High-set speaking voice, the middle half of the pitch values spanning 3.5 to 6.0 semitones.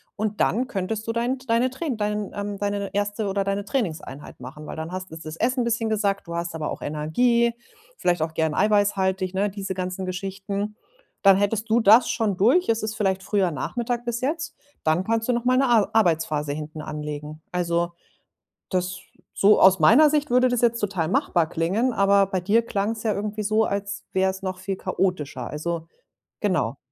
Yes: high, 200 Hz; average, 4.1 semitones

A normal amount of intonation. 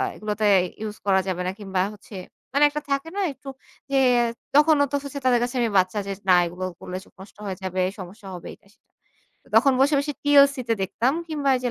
No: wide, 6.7 semitones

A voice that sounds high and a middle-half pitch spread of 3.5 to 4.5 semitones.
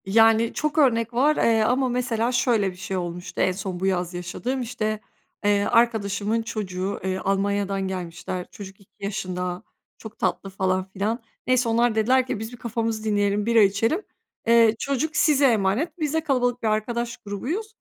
Yes: high, 220 Hz; average, 3.9 semitones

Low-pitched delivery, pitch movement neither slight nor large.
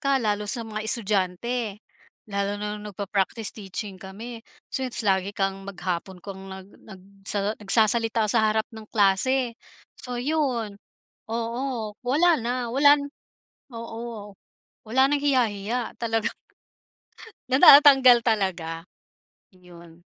No: high, 220 Hz; average, 3.6 semitones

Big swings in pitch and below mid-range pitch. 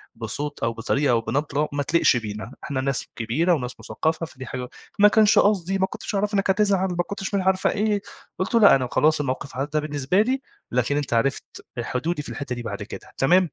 No: wide, 6.8 semitones; medium, 150 Hz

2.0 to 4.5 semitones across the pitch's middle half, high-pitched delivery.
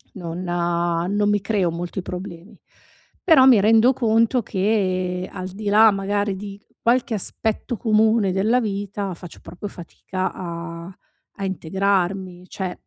Yes: average, 2.9 semitones; high, 195 Hz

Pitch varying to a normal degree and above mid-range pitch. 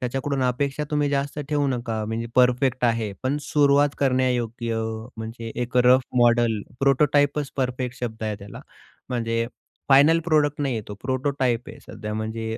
No: average, 3.3 semitones; low, 125 Hz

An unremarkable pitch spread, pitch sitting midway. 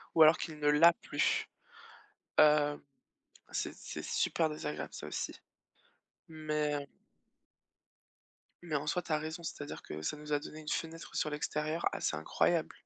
No: narrow, 1.2 semitones; medium, 150 Hz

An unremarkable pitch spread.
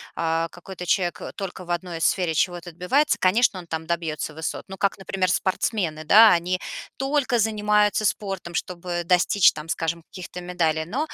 Yes: average, 3.3 semitones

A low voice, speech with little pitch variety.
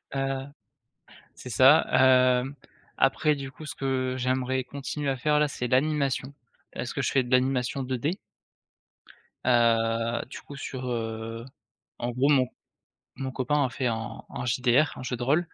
Yes: low, 130 Hz; narrow, 2.0 semitones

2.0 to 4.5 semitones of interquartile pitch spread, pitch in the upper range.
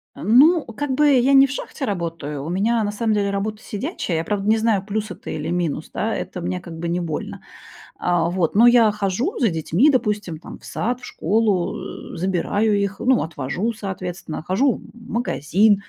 No: average, 5.1 semitones; high, 205 Hz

